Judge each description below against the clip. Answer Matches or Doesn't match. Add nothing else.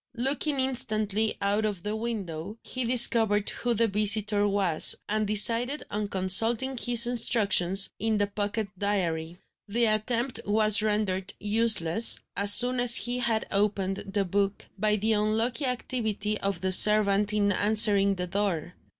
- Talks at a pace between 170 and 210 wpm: Doesn't match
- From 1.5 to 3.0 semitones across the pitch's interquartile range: Matches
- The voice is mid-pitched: Doesn't match